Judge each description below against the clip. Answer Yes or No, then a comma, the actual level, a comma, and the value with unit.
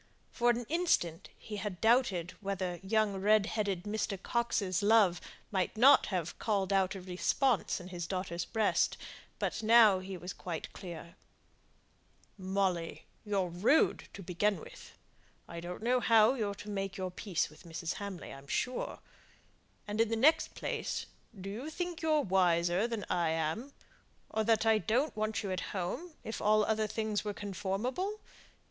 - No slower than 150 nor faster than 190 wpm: Yes, average, 160 wpm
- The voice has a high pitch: Yes, high, 200 Hz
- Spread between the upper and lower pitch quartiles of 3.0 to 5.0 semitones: Yes, average, 3.6 semitones